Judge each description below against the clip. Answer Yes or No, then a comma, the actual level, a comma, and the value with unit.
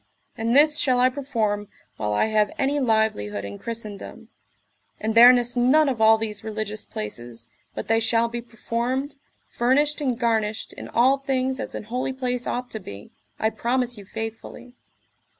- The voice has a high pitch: Yes, high, 230 Hz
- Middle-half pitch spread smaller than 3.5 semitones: Yes, average, 2.9 semitones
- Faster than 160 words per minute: Yes, average, 170 wpm